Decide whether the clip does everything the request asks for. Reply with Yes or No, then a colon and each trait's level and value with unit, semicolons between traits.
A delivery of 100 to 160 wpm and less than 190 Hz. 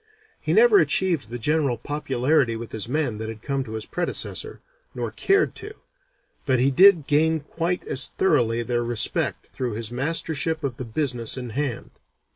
No: average, 170 wpm; low, 135 Hz